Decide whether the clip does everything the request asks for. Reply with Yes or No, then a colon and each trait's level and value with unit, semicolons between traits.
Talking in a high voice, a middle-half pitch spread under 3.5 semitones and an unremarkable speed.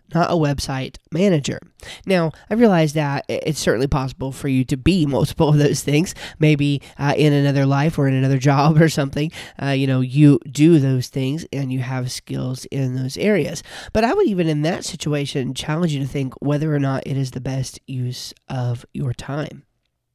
No: medium, 140 Hz; average, 2.8 semitones; average, 195 wpm